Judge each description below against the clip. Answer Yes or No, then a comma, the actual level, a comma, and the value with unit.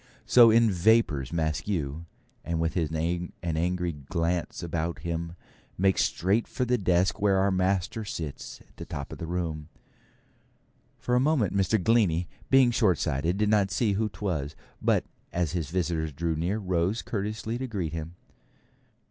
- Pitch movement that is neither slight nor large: Yes, average, 4.1 semitones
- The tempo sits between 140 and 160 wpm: Yes, average, 155 wpm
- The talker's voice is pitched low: Yes, very low, 90 Hz